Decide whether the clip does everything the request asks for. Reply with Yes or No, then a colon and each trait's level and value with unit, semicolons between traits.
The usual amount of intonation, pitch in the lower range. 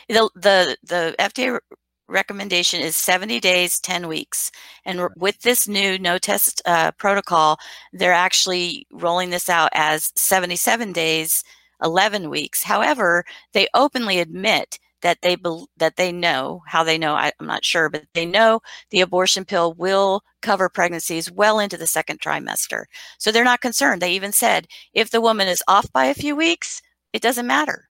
No: average, 4.1 semitones; medium, 185 Hz